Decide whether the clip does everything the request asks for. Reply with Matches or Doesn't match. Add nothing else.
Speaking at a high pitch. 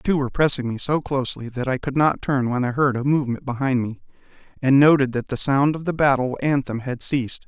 Doesn't match